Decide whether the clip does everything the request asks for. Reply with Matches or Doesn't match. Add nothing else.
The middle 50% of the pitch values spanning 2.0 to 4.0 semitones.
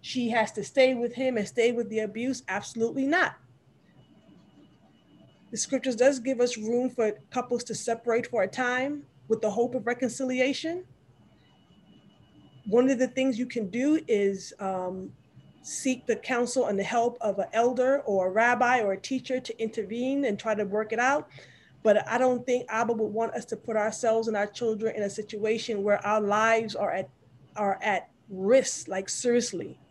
Matches